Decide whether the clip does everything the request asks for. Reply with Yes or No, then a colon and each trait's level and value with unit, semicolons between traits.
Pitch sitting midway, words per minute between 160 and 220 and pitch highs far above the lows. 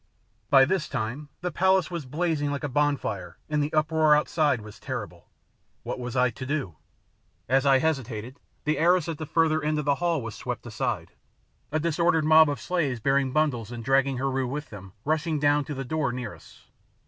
No: medium, 145 Hz; average, 195 wpm; average, 3.2 semitones